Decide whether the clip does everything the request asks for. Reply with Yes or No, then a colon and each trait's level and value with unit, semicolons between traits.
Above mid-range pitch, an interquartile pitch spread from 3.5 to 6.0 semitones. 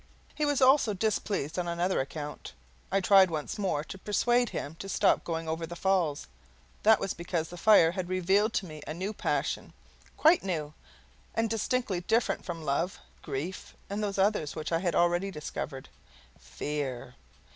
No: medium, 180 Hz; average, 4.5 semitones